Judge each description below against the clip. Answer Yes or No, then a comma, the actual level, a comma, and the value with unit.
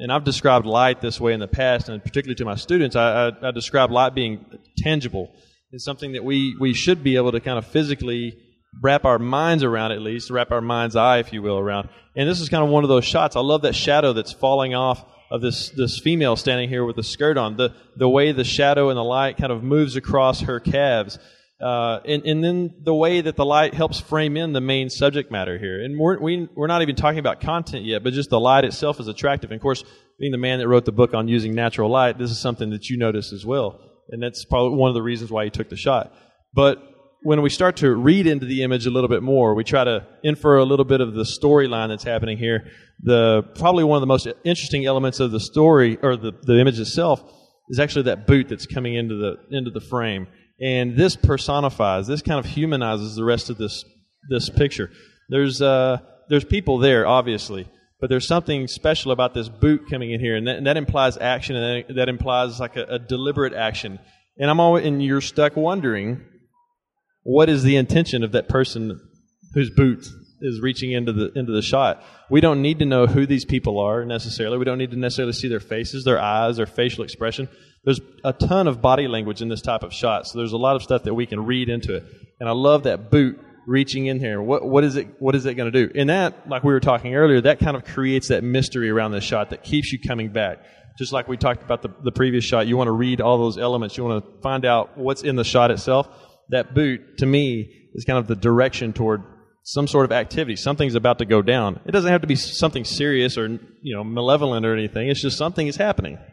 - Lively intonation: No, average, 3.2 semitones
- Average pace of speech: No, fast, 240 wpm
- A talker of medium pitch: No, low, 130 Hz